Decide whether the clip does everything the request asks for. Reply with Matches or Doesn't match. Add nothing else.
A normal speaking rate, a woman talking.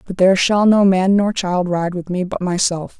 Doesn't match